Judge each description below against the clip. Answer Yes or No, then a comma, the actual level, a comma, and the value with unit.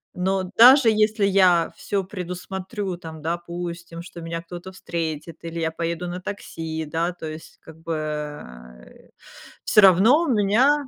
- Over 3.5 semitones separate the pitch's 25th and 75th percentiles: No, average, 3.2 semitones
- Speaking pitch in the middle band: Yes, medium, 175 Hz